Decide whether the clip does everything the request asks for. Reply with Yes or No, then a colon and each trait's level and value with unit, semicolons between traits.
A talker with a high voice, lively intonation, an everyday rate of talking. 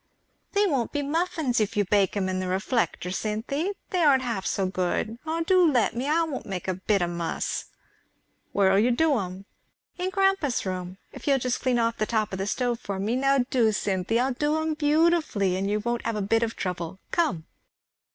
No: high, 230 Hz; wide, 7.0 semitones; fast, 210 wpm